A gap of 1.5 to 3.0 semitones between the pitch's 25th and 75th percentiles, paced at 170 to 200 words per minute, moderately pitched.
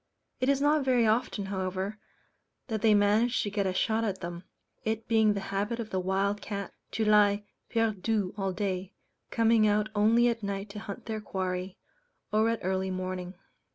No: narrow, 2.6 semitones; average, 180 wpm; high, 205 Hz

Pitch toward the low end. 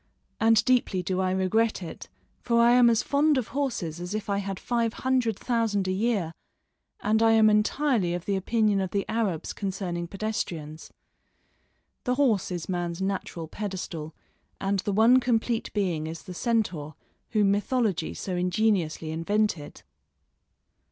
No: high, 200 Hz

